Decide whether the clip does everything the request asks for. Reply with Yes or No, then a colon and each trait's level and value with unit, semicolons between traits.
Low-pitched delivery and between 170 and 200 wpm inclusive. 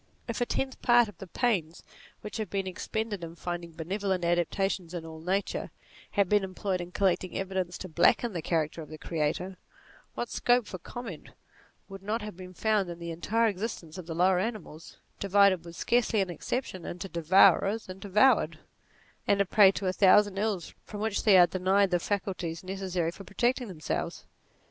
No: high, 190 Hz; average, 180 wpm